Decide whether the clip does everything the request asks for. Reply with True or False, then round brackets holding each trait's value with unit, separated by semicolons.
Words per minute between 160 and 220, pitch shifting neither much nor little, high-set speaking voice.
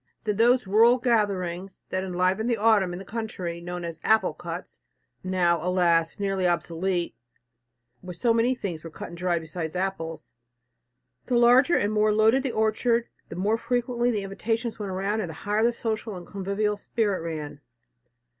True (170 wpm; 4.2 semitones; 195 Hz)